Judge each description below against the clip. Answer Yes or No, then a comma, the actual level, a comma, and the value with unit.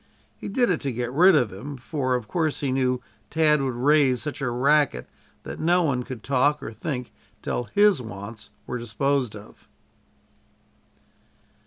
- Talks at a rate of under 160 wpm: No, average, 165 wpm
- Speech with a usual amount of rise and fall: Yes, average, 3.7 semitones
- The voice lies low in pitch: Yes, low, 130 Hz